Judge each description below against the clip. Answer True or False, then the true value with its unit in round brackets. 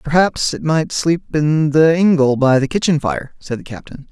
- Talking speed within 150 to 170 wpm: False (205 wpm)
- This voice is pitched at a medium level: True (150 Hz)